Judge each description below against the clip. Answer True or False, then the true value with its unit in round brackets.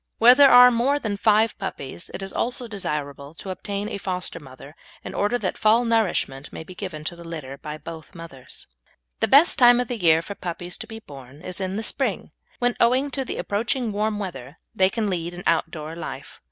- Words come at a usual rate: False (210 wpm)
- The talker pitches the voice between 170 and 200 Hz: True (190 Hz)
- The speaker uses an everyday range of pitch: False (5.9 semitones)